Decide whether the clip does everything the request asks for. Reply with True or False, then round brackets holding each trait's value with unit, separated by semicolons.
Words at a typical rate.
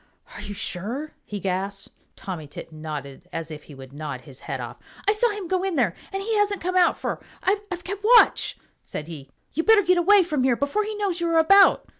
False (220 wpm)